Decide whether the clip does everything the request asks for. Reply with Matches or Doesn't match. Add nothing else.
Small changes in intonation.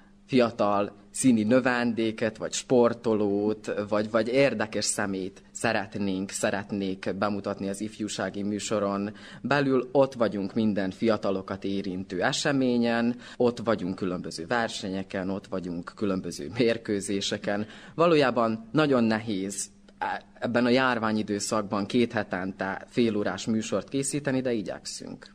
Doesn't match